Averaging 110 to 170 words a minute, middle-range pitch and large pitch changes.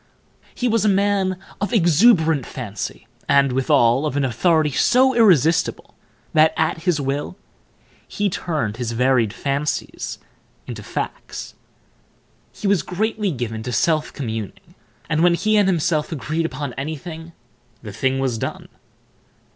Yes: slow, 135 wpm; medium, 155 Hz; wide, 5.8 semitones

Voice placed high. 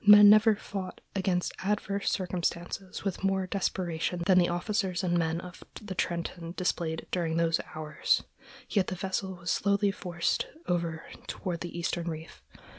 No: medium, 180 Hz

